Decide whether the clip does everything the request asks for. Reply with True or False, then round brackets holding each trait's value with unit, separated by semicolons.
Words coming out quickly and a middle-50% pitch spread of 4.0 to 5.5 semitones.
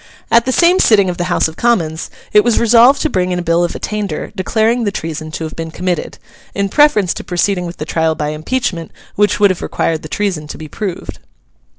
True (225 wpm; 4.9 semitones)